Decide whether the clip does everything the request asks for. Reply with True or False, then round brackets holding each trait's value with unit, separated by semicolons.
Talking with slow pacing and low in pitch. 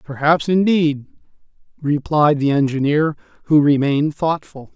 False (100 wpm; 150 Hz)